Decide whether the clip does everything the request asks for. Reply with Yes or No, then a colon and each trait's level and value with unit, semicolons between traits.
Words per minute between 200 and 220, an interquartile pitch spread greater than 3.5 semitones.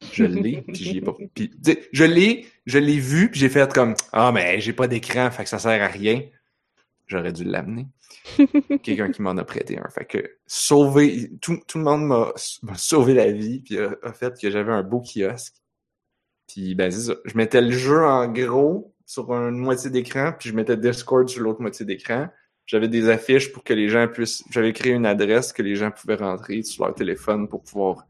Yes: average, 215 wpm; average, 4.4 semitones